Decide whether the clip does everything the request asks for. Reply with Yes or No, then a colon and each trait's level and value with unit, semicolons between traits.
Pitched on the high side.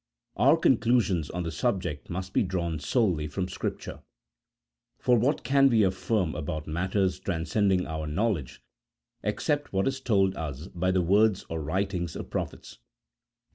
No: very low, 95 Hz